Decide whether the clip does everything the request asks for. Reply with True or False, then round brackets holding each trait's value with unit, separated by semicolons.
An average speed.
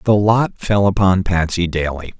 True (165 wpm)